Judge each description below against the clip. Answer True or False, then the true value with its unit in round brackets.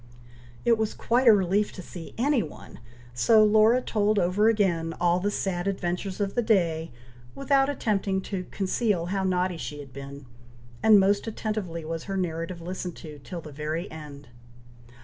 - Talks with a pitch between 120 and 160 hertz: False (190 Hz)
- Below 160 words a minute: False (170 wpm)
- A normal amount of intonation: True (4.3 semitones)